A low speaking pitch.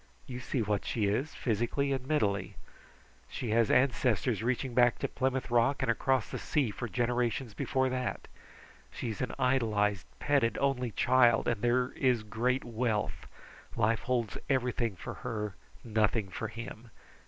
Yes: low, 120 Hz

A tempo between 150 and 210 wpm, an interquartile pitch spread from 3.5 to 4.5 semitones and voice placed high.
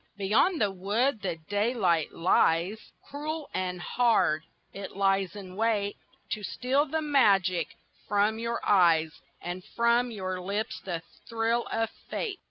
No: slow, 135 wpm; average, 4.2 semitones; high, 205 Hz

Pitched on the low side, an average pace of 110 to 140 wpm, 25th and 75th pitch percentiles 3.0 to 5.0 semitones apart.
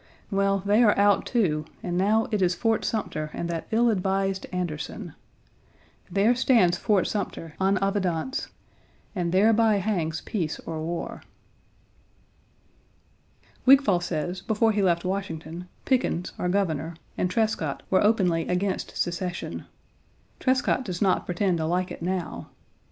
No: high, 190 Hz; slow, 135 wpm; average, 3.3 semitones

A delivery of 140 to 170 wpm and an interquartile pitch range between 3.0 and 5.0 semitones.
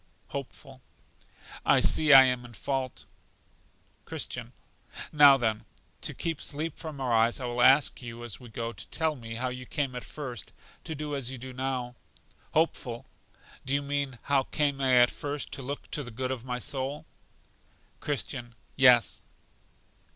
No: average, 165 wpm; narrow, 2.6 semitones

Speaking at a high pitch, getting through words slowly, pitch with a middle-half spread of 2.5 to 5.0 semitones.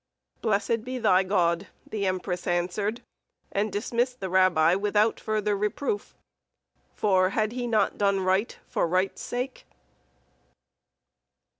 Yes: high, 200 Hz; slow, 120 wpm; average, 2.9 semitones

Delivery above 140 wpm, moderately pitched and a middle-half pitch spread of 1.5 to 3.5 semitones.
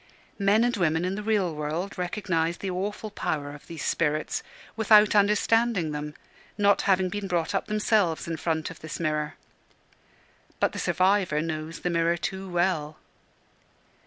No: average, 155 wpm; medium, 180 Hz; average, 4.2 semitones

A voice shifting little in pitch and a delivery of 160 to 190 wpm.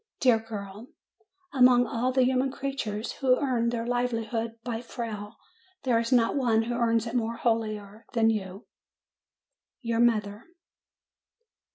No: narrow, 1.9 semitones; slow, 135 wpm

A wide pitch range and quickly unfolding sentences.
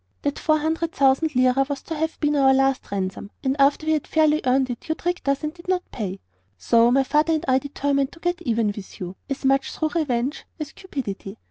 No: average, 3.6 semitones; fast, 225 wpm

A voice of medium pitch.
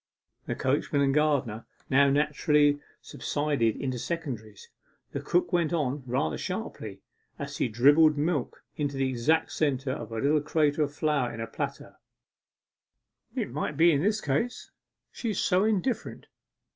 Yes: medium, 145 Hz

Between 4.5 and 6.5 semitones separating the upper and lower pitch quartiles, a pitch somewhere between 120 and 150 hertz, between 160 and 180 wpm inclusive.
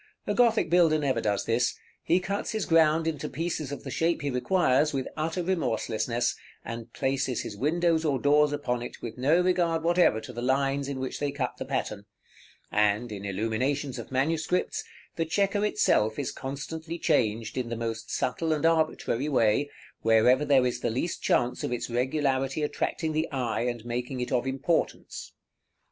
Yes: average, 5.0 semitones; low, 135 Hz; average, 175 wpm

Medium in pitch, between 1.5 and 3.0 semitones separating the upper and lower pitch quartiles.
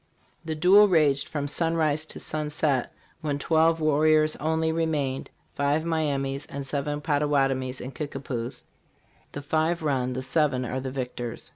Yes: medium, 145 Hz; average, 2.7 semitones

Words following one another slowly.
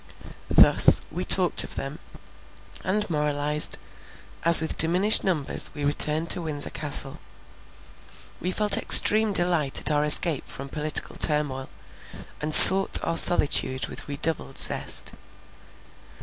Yes: slow, 120 wpm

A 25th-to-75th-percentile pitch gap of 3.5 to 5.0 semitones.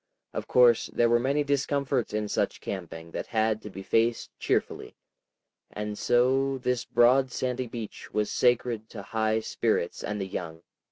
No: average, 3.0 semitones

